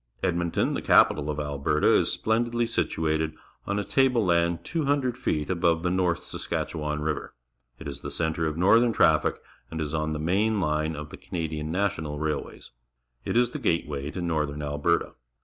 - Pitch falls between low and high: No, very low, 80 Hz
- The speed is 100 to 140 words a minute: No, average, 175 wpm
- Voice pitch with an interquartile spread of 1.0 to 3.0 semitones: No, average, 3.9 semitones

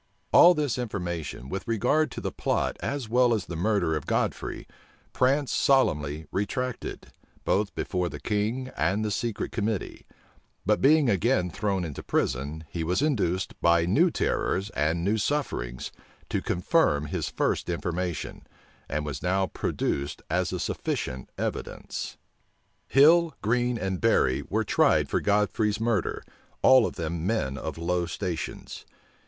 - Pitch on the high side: No, low, 100 Hz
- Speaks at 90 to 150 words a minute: Yes, average, 145 wpm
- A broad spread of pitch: Yes, wide, 6.5 semitones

